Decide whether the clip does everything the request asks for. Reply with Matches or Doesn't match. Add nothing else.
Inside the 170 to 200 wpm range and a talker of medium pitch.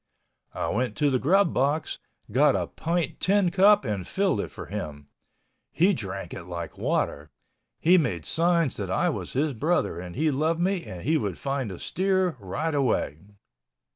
Matches